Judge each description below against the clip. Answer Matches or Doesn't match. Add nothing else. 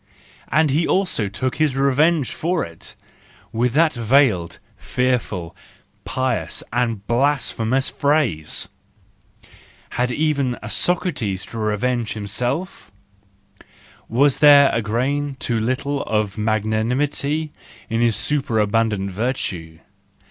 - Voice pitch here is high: Doesn't match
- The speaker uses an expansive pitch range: Doesn't match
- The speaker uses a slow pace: Matches